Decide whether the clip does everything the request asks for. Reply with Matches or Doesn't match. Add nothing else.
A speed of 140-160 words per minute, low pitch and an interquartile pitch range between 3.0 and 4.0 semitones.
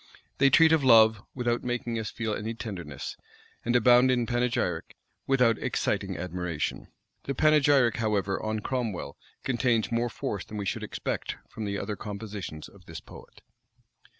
Matches